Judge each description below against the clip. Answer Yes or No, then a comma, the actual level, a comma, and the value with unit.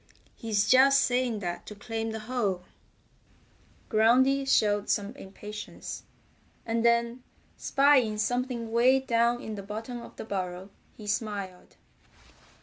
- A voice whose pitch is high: Yes, high, 225 Hz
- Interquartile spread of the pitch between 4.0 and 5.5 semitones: No, average, 3.1 semitones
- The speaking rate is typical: No, slow, 125 wpm